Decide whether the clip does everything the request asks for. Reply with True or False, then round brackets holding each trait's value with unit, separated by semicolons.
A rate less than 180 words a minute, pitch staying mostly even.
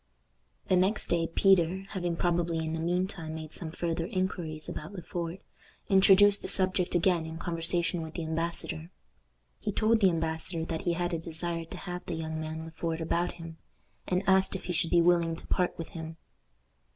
False (195 wpm; 1.9 semitones)